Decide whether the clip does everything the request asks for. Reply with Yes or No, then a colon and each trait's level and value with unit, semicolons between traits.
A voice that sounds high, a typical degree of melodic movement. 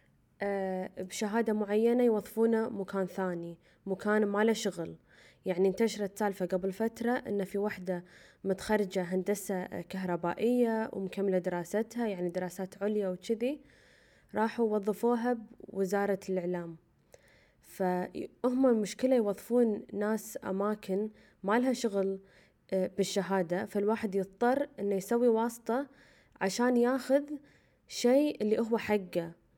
Yes: high, 205 Hz; average, 3.3 semitones